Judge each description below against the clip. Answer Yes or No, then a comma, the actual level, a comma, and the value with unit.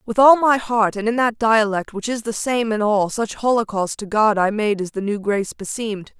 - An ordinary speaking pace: No, fast, 240 wpm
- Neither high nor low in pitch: No, high, 215 Hz